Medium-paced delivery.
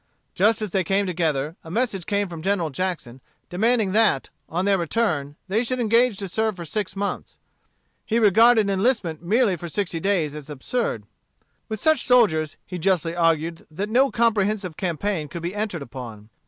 Yes: average, 170 wpm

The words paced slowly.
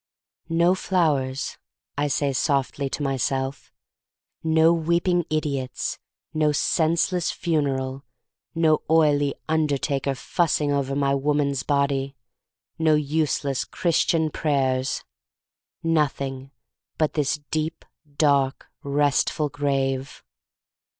Yes: slow, 90 wpm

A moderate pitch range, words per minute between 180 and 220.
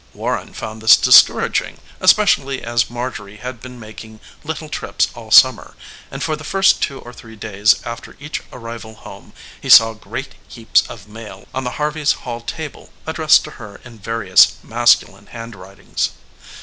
No: average, 3.7 semitones; average, 160 wpm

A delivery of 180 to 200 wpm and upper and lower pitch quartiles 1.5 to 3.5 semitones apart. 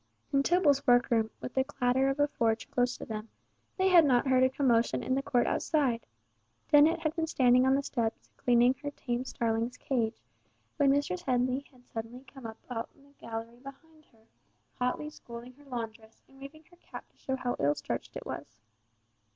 Yes: average, 190 wpm; average, 3.1 semitones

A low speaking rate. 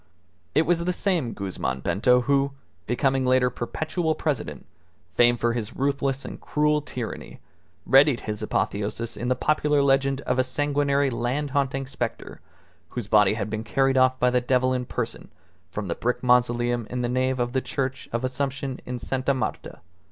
No: average, 170 wpm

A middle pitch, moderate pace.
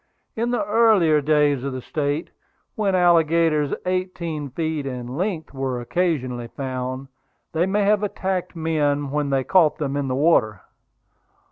Yes: medium, 155 Hz; average, 145 wpm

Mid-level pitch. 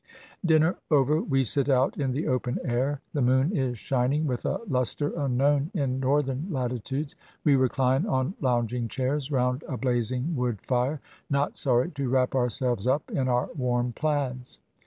No: low, 130 Hz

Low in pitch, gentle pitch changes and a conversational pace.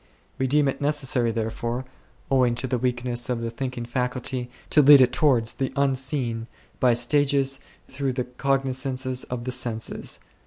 Yes: low, 130 Hz; narrow, 2.0 semitones; average, 160 wpm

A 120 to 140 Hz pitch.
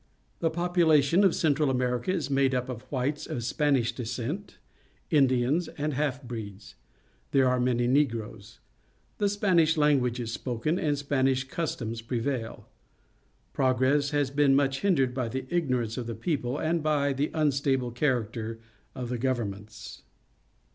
Yes: low, 135 Hz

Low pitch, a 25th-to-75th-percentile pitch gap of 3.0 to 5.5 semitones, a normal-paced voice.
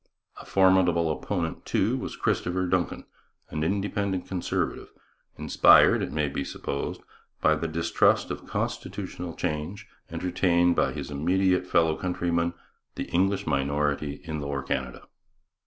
No: very low, 85 Hz; average, 3.4 semitones; slow, 125 wpm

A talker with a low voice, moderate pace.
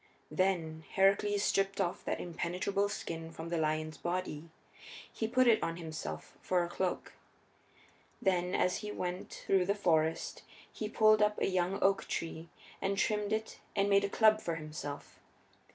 No: medium, 185 Hz; average, 160 wpm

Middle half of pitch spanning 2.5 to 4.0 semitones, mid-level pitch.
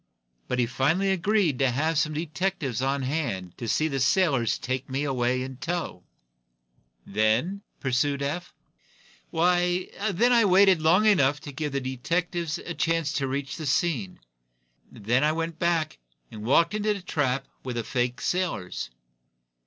No: average, 5.2 semitones; medium, 145 Hz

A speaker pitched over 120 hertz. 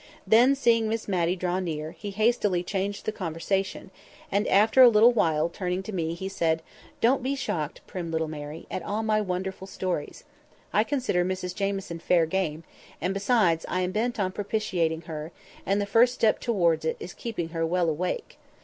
Yes: high, 190 Hz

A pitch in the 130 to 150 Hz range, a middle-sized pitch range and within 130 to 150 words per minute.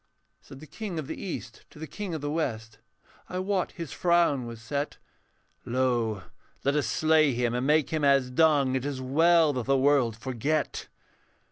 No: medium, 140 Hz; average, 3.9 semitones; average, 180 wpm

